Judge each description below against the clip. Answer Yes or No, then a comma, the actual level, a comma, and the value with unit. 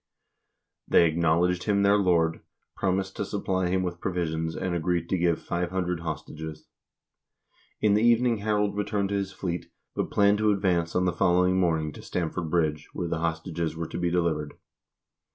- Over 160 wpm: Yes, average, 170 wpm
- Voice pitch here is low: Yes, very low, 90 Hz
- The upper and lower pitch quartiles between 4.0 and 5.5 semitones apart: No, average, 2.8 semitones